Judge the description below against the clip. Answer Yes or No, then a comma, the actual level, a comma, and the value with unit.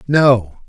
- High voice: No, low, 125 Hz